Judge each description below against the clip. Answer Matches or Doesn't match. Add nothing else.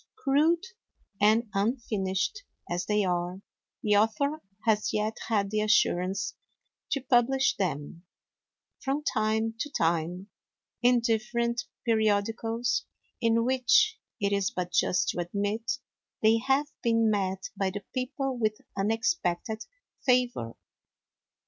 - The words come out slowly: Matches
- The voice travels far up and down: Doesn't match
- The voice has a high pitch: Matches